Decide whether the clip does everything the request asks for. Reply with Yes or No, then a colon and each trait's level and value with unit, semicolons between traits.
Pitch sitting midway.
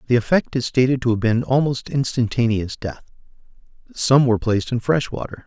No: low, 120 Hz